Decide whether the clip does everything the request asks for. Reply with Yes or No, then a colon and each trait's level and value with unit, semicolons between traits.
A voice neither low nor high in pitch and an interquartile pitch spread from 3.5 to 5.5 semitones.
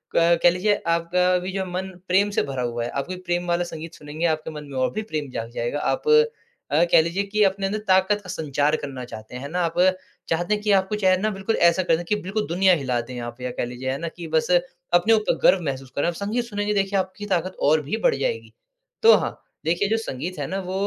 Yes: medium, 175 Hz; average, 4.6 semitones